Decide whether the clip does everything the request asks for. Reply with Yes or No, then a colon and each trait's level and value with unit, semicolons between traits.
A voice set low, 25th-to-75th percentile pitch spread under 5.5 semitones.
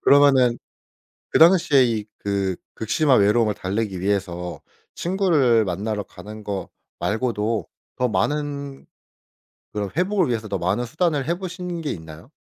No: low, 115 Hz; wide, 6.3 semitones